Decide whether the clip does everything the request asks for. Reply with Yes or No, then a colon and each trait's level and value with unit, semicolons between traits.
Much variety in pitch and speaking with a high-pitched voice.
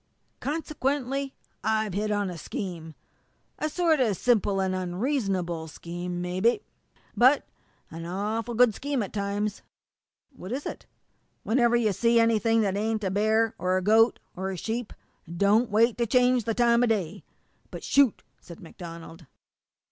No: average, 4.4 semitones; high, 215 Hz